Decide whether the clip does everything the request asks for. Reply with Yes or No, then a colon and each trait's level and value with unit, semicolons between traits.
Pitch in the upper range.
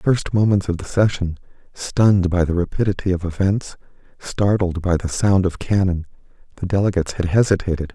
No: very low, 95 Hz